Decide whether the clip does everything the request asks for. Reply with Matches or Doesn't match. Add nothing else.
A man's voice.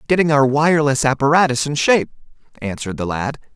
Matches